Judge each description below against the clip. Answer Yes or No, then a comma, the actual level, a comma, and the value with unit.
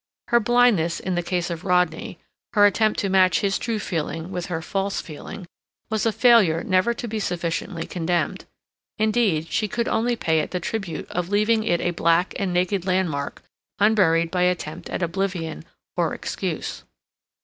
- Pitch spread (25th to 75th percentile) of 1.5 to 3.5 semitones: No, average, 3.9 semitones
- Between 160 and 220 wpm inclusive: Yes, average, 170 wpm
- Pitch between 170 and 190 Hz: Yes, medium, 185 Hz